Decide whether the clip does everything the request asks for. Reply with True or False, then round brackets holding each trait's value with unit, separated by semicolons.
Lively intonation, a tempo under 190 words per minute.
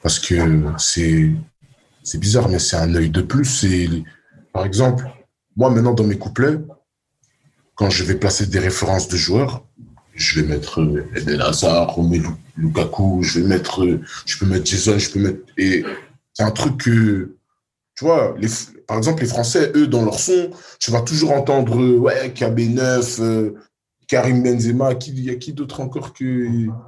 True (5.7 semitones; 165 wpm)